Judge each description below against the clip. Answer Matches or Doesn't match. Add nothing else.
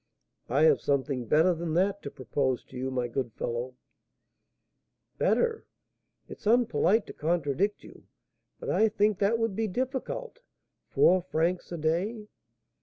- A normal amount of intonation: Doesn't match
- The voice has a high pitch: Doesn't match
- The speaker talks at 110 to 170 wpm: Matches